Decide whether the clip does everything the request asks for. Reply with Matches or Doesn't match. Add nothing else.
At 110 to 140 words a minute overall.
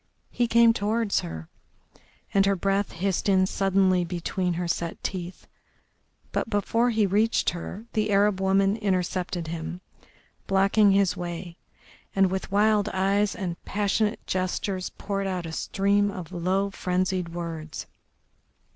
Matches